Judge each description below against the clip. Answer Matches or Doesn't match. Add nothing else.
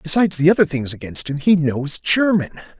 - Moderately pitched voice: Matches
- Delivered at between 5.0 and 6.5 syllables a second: Matches